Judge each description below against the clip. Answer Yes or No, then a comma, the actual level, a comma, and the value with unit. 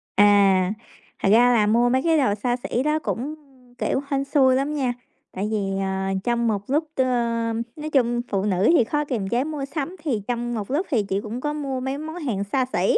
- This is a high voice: Yes, high, 245 Hz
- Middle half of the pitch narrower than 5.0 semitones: No, average, 5.3 semitones